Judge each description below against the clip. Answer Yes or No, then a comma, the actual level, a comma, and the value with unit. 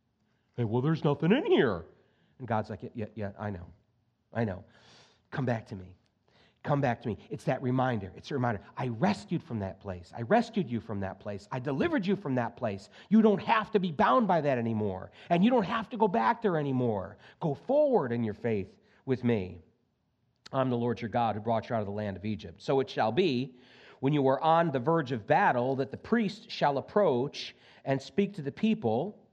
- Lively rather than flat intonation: Yes, wide, 6.6 semitones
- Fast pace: Yes, fast, 220 wpm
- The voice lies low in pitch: Yes, low, 125 Hz